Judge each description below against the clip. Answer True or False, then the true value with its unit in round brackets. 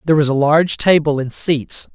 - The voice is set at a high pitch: False (150 Hz)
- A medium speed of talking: False (215 wpm)